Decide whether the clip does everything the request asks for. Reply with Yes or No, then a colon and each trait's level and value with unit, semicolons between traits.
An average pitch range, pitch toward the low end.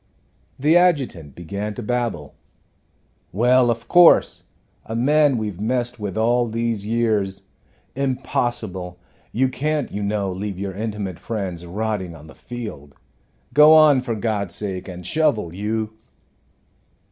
Yes: average, 4.3 semitones; low, 110 Hz